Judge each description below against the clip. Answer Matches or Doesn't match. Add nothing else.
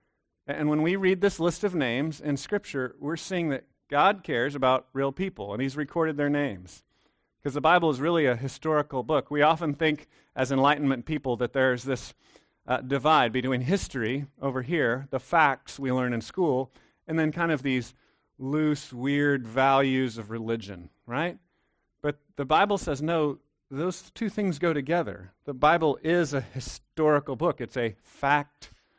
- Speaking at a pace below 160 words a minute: Doesn't match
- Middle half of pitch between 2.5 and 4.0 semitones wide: Matches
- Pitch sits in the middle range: Matches